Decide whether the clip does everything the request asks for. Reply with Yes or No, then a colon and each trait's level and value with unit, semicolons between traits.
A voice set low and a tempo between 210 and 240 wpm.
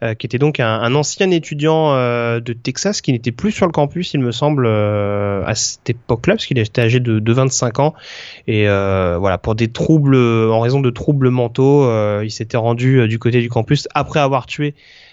Yes: low, 125 Hz; fast, 220 wpm